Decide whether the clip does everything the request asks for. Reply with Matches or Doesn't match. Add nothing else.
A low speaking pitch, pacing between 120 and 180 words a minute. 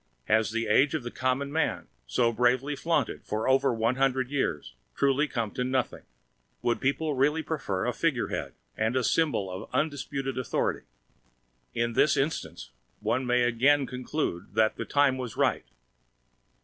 Matches